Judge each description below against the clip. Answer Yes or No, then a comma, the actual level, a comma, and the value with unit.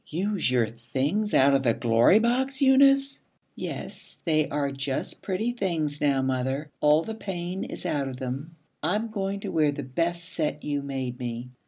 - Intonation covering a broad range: Yes, wide, 6.8 semitones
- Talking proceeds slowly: No, average, 175 wpm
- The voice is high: No, medium, 150 Hz